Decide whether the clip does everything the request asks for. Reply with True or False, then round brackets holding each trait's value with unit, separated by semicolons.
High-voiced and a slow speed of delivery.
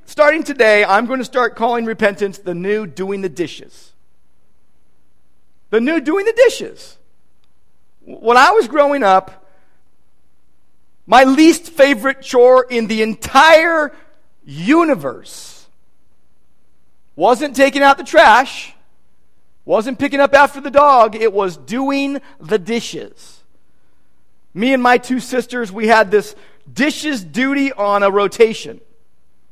True (220 Hz; 120 wpm)